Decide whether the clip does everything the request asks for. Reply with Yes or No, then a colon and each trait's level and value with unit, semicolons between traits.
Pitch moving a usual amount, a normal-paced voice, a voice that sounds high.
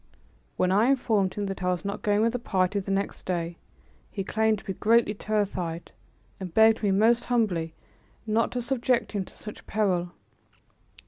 Yes: average, 3.1 semitones; average, 180 wpm; high, 205 Hz